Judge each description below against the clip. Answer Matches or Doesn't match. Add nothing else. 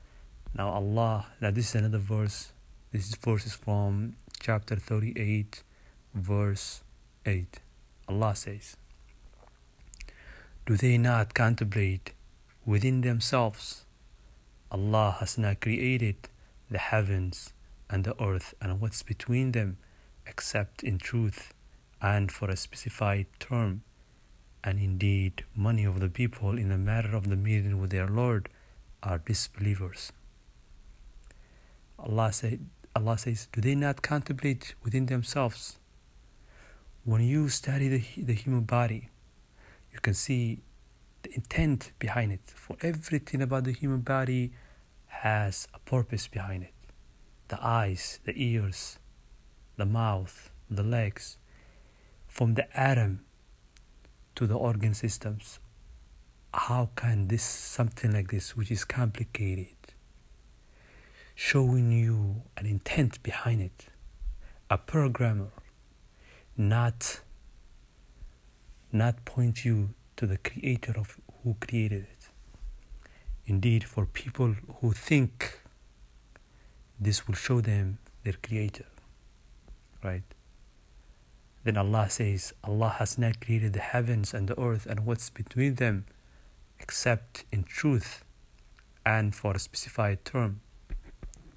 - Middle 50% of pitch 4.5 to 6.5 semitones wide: Doesn't match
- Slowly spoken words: Matches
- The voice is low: Matches